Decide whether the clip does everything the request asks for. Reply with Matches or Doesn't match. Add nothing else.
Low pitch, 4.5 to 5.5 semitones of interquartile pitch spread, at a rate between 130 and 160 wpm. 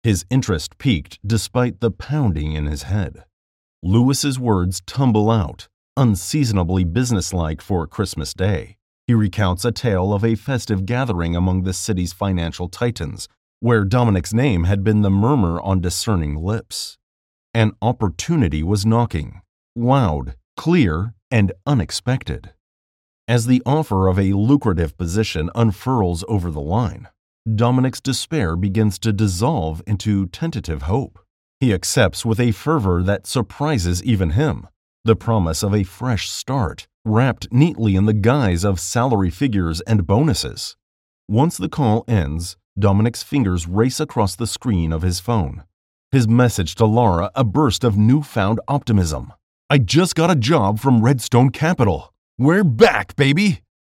Matches